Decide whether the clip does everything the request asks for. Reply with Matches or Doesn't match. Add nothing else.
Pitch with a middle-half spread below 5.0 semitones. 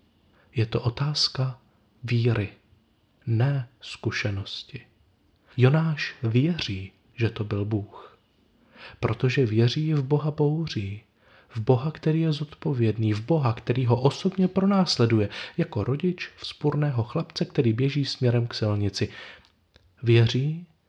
Doesn't match